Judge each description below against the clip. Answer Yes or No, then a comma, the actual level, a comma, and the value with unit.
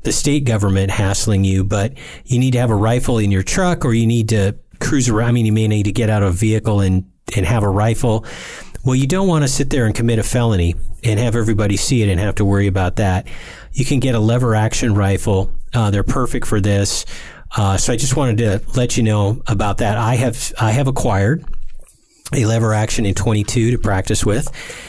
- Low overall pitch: Yes, low, 110 Hz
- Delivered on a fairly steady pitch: No, average, 3.5 semitones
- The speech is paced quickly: Yes, fast, 230 wpm